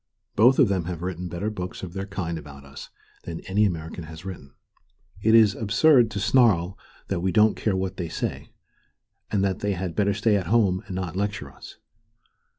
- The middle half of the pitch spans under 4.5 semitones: Yes, average, 3.2 semitones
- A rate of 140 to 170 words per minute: No, average, 195 wpm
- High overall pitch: No, very low, 95 Hz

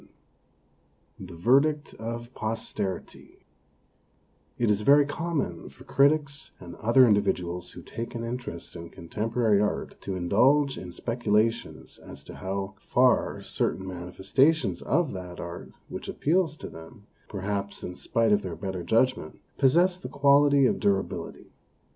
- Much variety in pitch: Yes, wide, 6.5 semitones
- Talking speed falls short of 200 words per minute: Yes, average, 140 wpm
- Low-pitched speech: Yes, low, 115 Hz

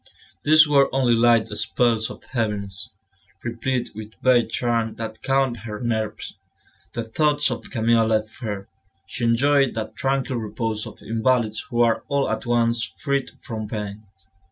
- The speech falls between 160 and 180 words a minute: No, average, 150 wpm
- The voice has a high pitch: No, low, 115 Hz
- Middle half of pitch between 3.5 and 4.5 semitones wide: No, average, 2.8 semitones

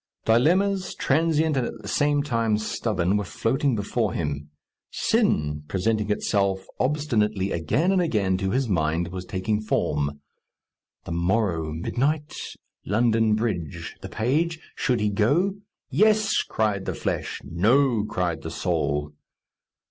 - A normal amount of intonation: No, wide, 7.2 semitones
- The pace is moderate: No, slow, 130 wpm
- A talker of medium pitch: No, low, 110 Hz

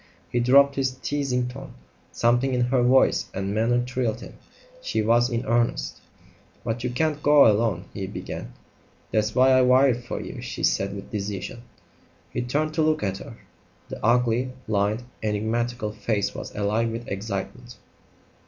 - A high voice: No, low, 120 Hz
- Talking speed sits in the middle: Yes, average, 160 wpm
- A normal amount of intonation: Yes, average, 3.0 semitones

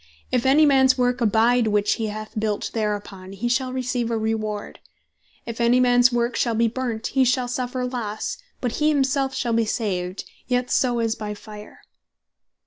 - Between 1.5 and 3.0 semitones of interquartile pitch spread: Yes, average, 2.7 semitones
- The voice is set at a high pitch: Yes, high, 235 Hz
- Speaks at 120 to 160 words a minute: No, average, 175 wpm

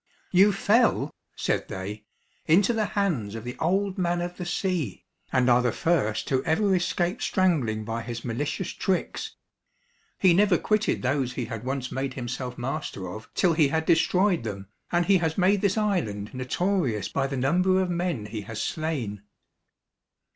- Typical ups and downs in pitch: No, wide, 7.4 semitones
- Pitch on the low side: No, medium, 155 Hz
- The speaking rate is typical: Yes, average, 170 wpm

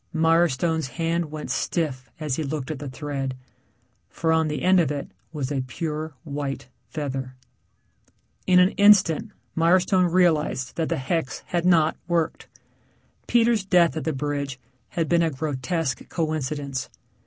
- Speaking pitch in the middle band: Yes, medium, 155 Hz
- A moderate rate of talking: Yes, average, 145 wpm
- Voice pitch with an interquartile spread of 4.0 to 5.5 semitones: No, average, 3.4 semitones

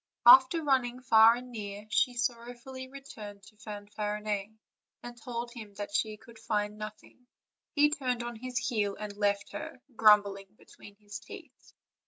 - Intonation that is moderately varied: Yes, average, 3.1 semitones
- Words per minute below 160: Yes, average, 150 wpm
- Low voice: No, high, 220 Hz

